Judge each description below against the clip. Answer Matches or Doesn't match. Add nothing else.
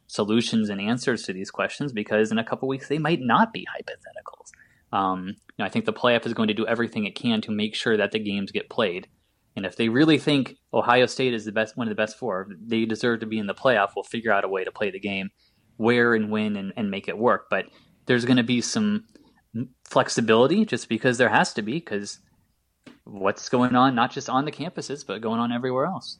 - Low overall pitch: Matches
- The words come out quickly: Matches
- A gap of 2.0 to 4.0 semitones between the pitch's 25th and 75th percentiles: Matches